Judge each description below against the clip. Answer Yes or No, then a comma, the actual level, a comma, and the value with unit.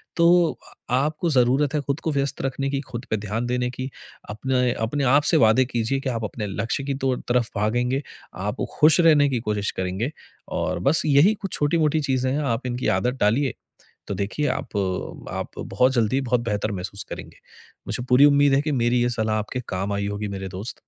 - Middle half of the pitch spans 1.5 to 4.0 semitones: No, average, 4.5 semitones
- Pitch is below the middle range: Yes, low, 125 Hz